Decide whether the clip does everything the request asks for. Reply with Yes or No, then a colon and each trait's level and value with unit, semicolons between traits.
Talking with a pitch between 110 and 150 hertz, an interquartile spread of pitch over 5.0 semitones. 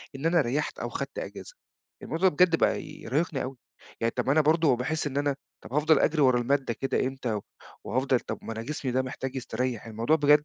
No: low, 135 Hz; average, 3.3 semitones